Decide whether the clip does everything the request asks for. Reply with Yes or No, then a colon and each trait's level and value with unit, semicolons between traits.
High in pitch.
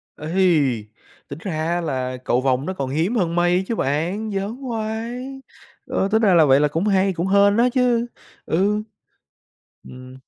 No: medium, 180 Hz